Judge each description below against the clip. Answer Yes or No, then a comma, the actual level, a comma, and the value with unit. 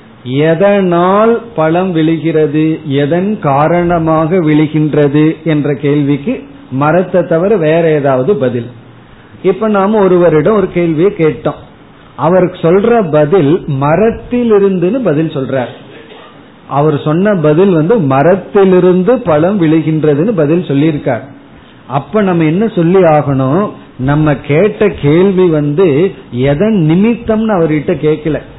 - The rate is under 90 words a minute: No, average, 95 wpm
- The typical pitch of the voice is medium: Yes, medium, 160 Hz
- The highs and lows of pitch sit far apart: No, average, 4.2 semitones